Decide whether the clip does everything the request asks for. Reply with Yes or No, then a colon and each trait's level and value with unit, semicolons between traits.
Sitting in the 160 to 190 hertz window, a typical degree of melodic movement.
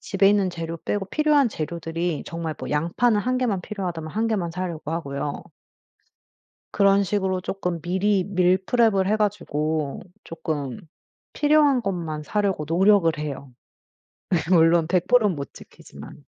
Yes: medium, 185 Hz; average, 4.1 semitones